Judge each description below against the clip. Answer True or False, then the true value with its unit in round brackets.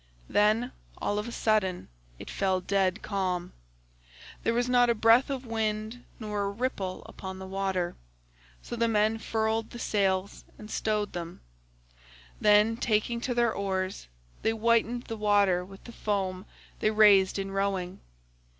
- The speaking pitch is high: True (210 Hz)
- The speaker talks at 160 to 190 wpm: False (150 wpm)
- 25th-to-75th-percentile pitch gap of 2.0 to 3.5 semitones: True (2.9 semitones)